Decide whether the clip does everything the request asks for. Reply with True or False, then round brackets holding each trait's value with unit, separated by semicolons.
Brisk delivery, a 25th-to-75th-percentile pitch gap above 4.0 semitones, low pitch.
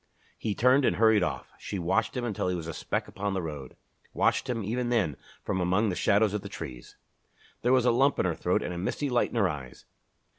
True (235 wpm; 5.2 semitones; 100 Hz)